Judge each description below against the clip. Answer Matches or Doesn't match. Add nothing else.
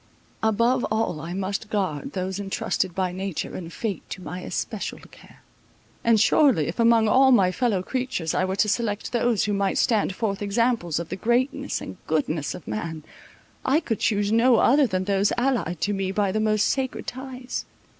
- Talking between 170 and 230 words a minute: Matches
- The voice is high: Matches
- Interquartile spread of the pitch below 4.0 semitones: Doesn't match